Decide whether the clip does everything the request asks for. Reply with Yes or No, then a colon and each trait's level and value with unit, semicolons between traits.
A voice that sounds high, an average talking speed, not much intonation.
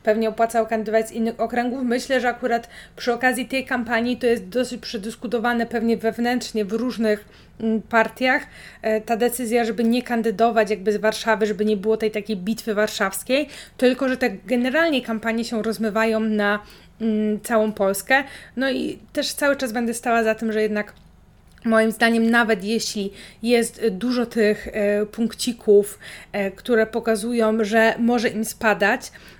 Yes: high, 225 Hz; average, 145 wpm; narrow, 1.8 semitones